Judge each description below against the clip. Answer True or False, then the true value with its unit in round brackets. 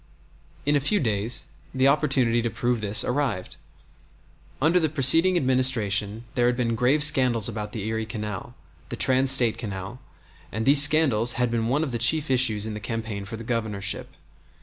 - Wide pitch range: False (3.7 semitones)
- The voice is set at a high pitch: False (120 Hz)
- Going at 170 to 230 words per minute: True (175 wpm)